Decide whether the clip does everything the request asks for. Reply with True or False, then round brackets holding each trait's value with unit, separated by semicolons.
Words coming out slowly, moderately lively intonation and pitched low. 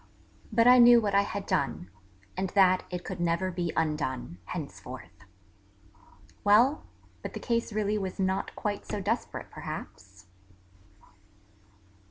False (130 wpm; 3.6 semitones; 190 Hz)